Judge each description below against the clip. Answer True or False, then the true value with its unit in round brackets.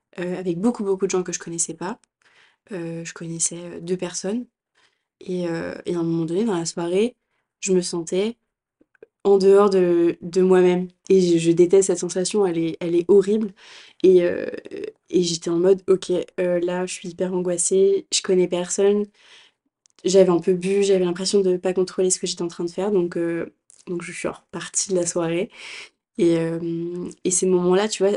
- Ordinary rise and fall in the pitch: False (2.0 semitones)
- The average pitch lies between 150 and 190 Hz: True (185 Hz)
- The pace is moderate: True (200 wpm)